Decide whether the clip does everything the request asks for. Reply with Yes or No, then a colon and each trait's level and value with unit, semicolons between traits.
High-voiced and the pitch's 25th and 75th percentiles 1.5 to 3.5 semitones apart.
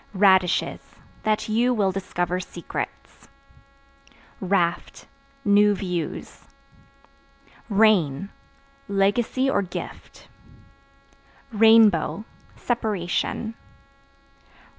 Yes: high, 200 Hz; average, 3.2 semitones